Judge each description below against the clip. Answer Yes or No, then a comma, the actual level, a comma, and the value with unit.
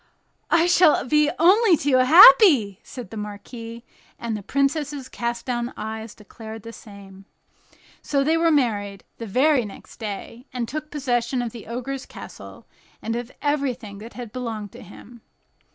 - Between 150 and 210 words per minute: Yes, average, 155 wpm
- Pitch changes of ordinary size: Yes, average, 4.2 semitones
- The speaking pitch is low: No, high, 240 Hz